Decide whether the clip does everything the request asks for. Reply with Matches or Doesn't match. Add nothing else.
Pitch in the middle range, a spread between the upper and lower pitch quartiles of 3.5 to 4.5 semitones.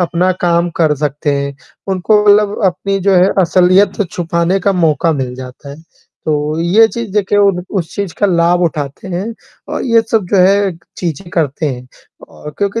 Matches